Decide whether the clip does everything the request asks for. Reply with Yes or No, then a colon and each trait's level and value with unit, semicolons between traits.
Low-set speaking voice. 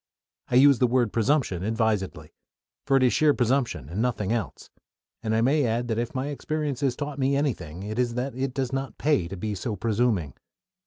Yes: low, 120 Hz